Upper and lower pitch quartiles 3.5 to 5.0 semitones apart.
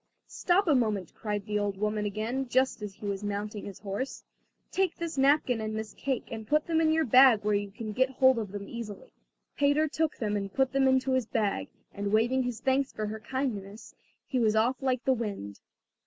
Yes: average, 4.2 semitones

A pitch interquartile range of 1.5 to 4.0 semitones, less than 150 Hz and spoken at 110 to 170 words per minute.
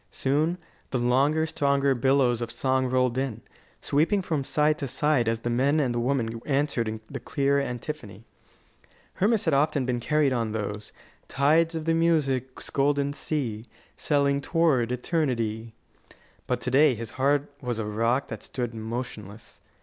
Yes: average, 3.7 semitones; low, 135 Hz; average, 155 wpm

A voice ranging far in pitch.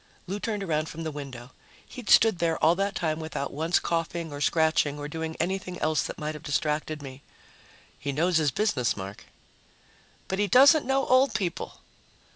No: average, 4.3 semitones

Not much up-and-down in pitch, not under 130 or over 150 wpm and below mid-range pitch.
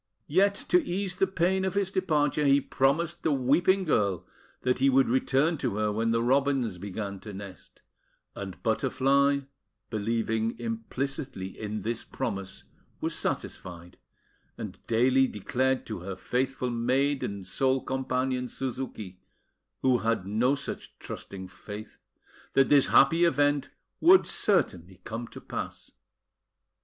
No: average, 4.8 semitones; slow, 135 wpm; low, 130 Hz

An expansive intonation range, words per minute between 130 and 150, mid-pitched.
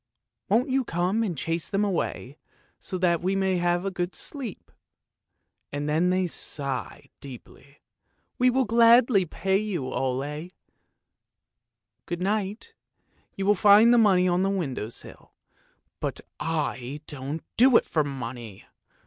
Yes: wide, 6.0 semitones; average, 145 wpm; medium, 180 Hz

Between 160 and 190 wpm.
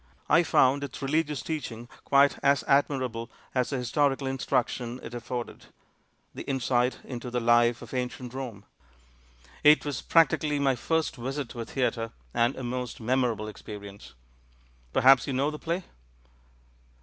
No: average, 150 wpm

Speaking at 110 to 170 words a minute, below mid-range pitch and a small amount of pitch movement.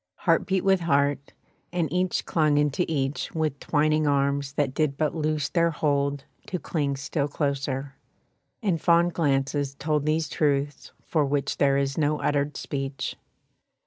No: average, 150 wpm; medium, 145 Hz; narrow, 2.1 semitones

